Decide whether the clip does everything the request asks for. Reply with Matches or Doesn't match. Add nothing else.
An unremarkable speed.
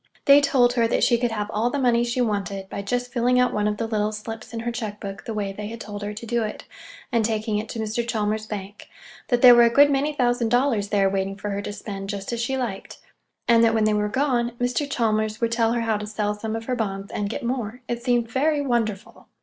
Doesn't match